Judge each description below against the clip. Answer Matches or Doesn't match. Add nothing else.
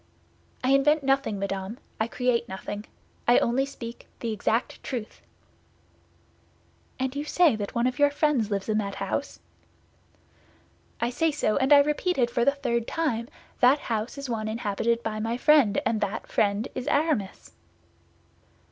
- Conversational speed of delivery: Matches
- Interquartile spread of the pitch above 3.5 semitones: Matches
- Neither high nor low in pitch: Doesn't match